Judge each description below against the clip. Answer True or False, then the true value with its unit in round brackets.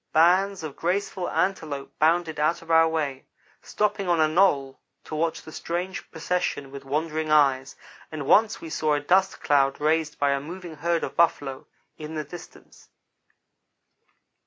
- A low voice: False (160 Hz)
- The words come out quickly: False (160 wpm)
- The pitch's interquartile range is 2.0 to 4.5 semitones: True (3.2 semitones)